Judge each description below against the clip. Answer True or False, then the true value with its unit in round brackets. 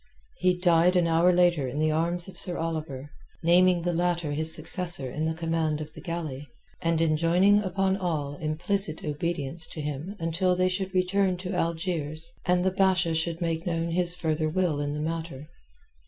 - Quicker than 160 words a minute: True (185 wpm)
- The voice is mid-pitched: True (165 Hz)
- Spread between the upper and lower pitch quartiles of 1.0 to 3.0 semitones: True (2.4 semitones)